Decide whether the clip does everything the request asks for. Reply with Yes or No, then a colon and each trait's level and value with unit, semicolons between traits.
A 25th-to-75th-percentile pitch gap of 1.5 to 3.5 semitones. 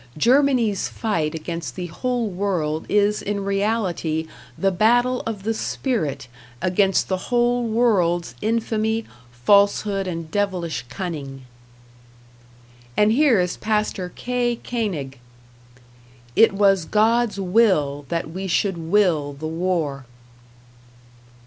No: average, 5.0 semitones